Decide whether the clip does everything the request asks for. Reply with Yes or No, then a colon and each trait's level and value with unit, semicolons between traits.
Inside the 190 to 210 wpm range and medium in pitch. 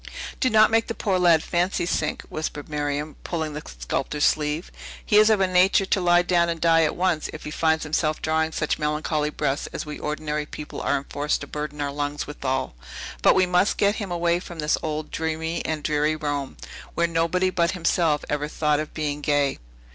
Yes: average, 200 wpm; medium, 155 Hz